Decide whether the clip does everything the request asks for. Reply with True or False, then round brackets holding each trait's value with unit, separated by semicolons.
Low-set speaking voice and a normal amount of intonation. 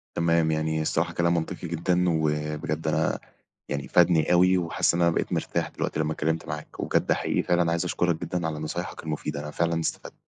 False (80 Hz; 1.7 semitones)